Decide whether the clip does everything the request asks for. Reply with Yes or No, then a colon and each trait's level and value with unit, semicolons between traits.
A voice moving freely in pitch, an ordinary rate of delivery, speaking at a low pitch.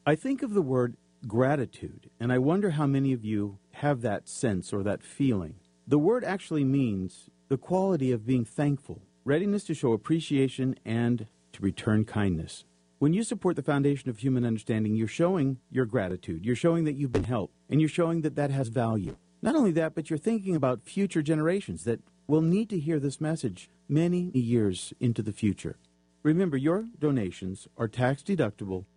Yes: wide, 7.0 semitones; average, 180 wpm; low, 130 Hz